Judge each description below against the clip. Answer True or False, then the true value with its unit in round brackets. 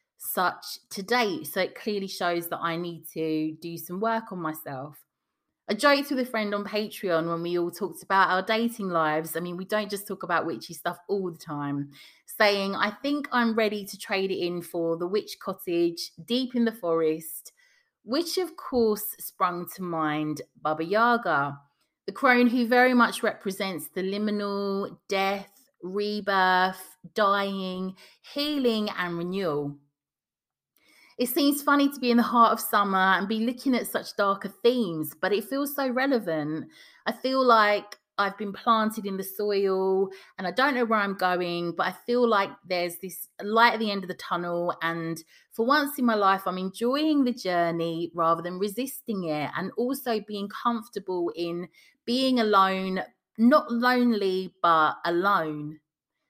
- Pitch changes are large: False (5.0 semitones)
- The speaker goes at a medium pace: True (170 wpm)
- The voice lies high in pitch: True (195 Hz)